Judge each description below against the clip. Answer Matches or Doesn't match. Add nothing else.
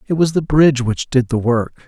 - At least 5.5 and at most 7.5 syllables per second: Doesn't match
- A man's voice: Matches